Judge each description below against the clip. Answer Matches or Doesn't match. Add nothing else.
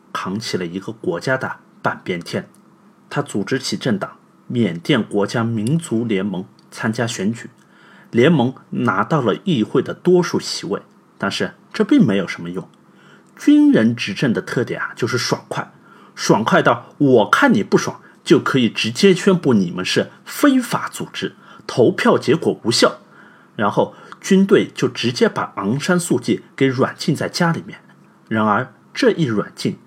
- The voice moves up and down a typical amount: Doesn't match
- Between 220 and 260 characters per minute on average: Matches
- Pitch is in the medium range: Matches